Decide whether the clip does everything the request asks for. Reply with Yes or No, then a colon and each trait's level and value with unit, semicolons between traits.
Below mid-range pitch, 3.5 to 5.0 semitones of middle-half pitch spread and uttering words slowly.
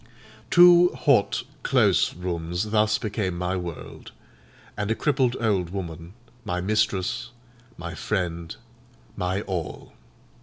Yes: very low, 95 Hz; average, 3.8 semitones; slow, 110 wpm